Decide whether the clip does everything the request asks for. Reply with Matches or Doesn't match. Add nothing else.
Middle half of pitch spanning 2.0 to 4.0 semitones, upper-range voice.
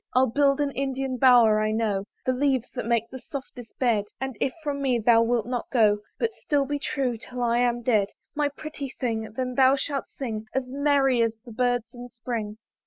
Matches